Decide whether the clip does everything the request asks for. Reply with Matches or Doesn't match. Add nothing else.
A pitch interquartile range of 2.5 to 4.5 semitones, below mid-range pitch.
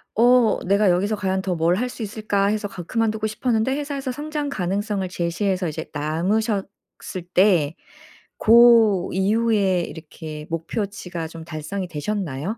Doesn't match